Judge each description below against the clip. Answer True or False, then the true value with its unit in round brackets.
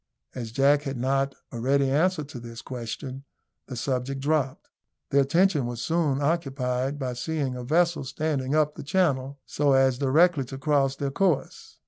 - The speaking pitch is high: False (135 Hz)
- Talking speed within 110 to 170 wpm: True (165 wpm)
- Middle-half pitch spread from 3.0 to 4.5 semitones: False (2.5 semitones)